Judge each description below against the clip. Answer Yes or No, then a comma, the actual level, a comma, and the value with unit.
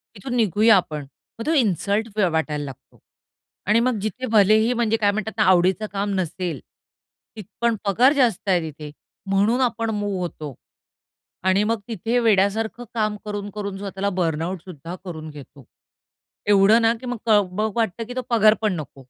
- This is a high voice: Yes, high, 205 Hz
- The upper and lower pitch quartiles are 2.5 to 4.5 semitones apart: Yes, average, 3.7 semitones